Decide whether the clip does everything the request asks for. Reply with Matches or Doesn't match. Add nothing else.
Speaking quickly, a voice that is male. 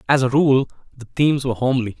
Matches